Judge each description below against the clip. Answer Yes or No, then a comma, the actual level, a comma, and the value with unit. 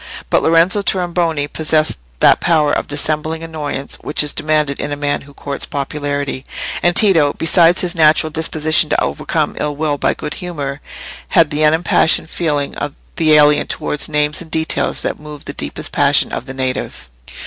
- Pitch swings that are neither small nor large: No, narrow, 1.9 semitones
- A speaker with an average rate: Yes, average, 170 wpm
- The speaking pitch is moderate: Yes, medium, 150 Hz